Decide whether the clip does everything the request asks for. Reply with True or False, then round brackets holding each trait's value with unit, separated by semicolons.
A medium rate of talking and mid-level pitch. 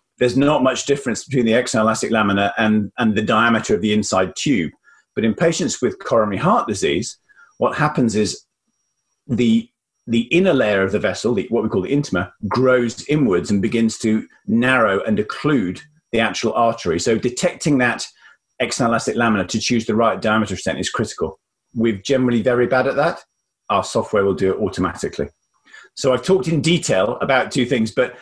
False (175 wpm; 115 Hz)